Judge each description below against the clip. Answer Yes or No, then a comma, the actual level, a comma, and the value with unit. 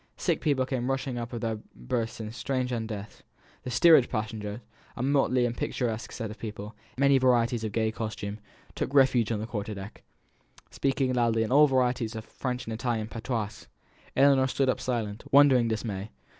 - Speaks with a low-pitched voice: Yes, low, 120 Hz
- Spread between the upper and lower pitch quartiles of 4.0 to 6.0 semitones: No, average, 2.9 semitones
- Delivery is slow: No, average, 185 wpm